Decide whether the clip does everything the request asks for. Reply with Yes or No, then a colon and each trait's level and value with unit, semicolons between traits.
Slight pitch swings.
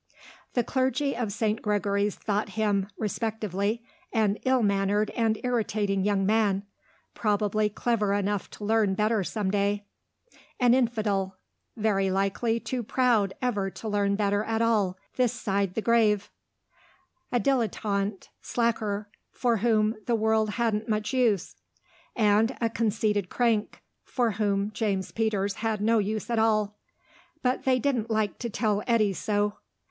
Yes: narrow, 2.2 semitones